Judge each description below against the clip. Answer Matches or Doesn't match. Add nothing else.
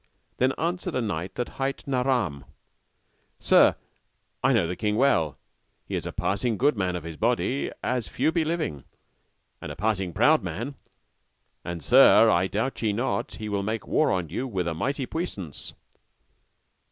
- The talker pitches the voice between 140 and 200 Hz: Doesn't match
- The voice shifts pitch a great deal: Matches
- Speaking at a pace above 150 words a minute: Matches